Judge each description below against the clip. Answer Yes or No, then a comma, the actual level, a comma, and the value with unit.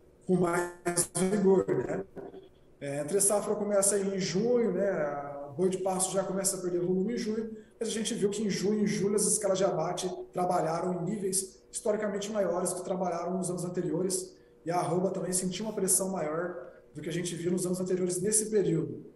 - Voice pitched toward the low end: No, medium, 185 Hz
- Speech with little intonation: Yes, narrow, 2.3 semitones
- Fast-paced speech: Yes, fast, 205 wpm